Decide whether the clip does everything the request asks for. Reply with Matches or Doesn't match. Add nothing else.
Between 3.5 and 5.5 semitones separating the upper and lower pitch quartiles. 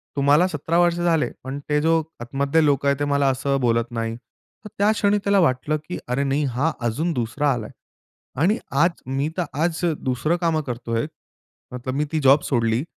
Matches